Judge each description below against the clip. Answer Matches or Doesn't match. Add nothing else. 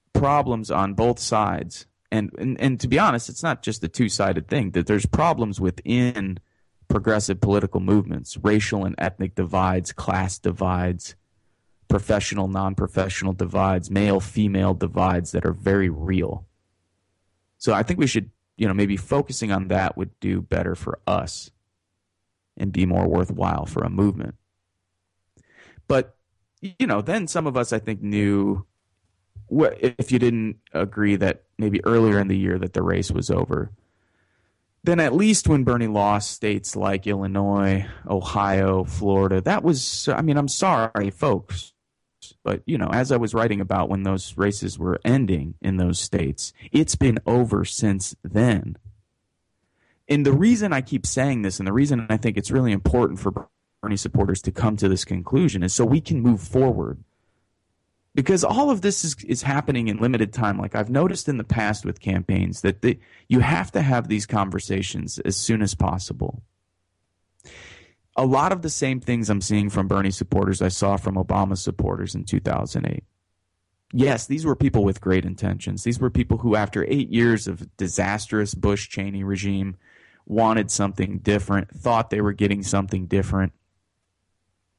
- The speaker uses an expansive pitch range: Doesn't match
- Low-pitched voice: Matches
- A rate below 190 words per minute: Matches